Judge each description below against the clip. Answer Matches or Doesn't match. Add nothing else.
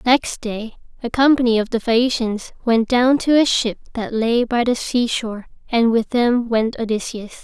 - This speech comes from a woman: Matches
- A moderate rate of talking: Matches